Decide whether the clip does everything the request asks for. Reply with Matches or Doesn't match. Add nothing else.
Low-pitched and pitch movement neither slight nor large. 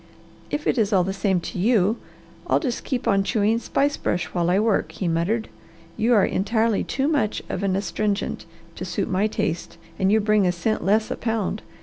Doesn't match